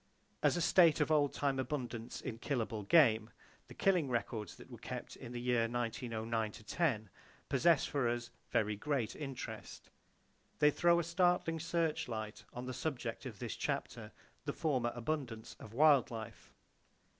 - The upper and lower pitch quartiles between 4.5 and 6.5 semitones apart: Yes, average, 5.1 semitones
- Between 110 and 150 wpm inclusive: Yes, average, 145 wpm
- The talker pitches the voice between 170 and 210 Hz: No, low, 125 Hz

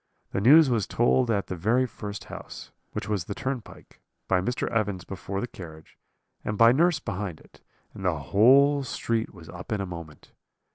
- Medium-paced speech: Yes, average, 190 wpm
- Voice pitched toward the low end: Yes, low, 105 Hz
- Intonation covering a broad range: No, average, 4.9 semitones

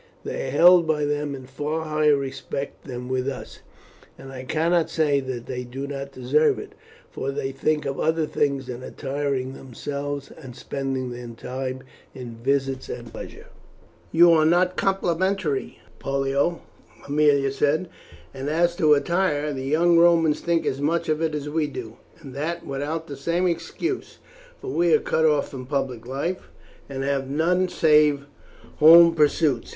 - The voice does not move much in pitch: No, average, 3.2 semitones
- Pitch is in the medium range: Yes, medium, 145 Hz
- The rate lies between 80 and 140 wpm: No, average, 165 wpm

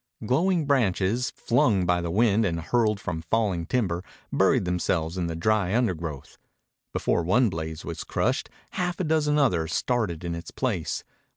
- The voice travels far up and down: Yes, wide, 6.3 semitones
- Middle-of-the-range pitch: No, very low, 95 Hz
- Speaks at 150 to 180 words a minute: Yes, average, 160 wpm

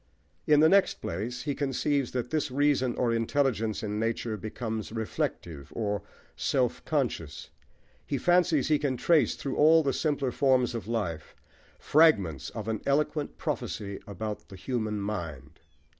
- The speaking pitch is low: Yes, low, 120 Hz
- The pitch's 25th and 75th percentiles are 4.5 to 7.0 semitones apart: Yes, average, 5.2 semitones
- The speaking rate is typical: Yes, average, 145 wpm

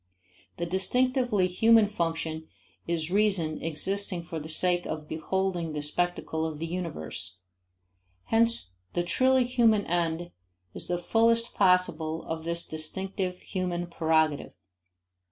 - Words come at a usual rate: No, slow, 120 wpm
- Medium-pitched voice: Yes, medium, 175 Hz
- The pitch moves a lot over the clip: No, average, 3.6 semitones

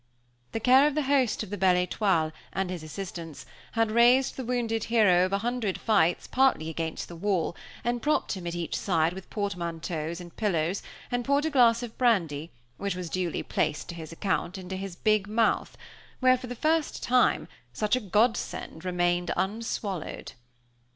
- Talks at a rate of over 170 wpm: Yes, average, 180 wpm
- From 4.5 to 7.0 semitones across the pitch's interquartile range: Yes, wide, 5.4 semitones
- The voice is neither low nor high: No, high, 200 Hz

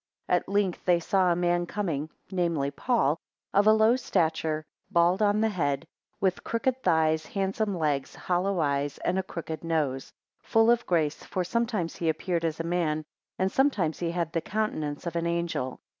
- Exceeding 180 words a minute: No, average, 175 wpm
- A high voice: No, medium, 175 Hz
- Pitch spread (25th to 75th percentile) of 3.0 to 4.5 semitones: Yes, average, 3.9 semitones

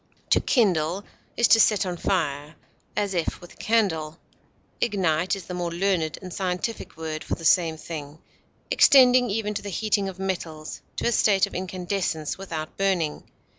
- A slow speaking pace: No, average, 170 wpm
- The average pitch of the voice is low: No, medium, 185 Hz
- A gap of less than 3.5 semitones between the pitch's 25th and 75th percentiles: No, average, 3.8 semitones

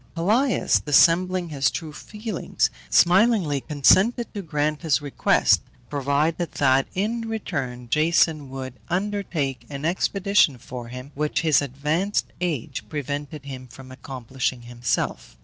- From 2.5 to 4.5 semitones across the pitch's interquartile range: No, average, 5.1 semitones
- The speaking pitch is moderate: Yes, medium, 150 Hz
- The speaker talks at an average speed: No, slow, 120 wpm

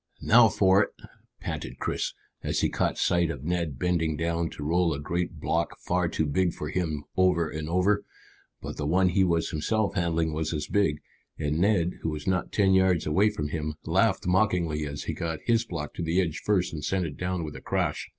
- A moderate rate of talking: No, fast, 210 wpm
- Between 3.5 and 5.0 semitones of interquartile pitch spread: No, average, 3.0 semitones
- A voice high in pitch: No, very low, 85 Hz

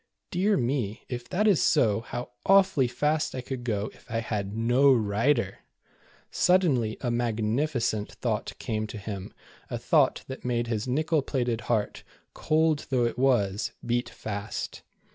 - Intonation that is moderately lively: Yes, average, 4.4 semitones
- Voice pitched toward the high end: No, low, 120 Hz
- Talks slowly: No, average, 160 wpm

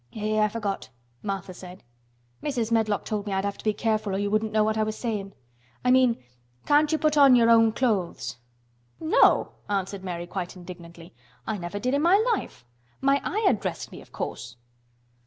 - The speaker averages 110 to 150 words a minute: No, average, 190 wpm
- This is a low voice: No, high, 215 Hz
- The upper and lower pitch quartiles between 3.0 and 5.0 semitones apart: Yes, average, 3.6 semitones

